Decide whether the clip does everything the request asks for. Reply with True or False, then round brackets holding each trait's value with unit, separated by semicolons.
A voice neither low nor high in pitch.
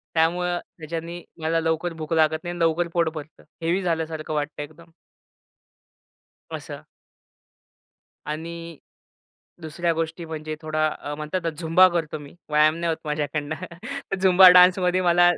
True (165 Hz)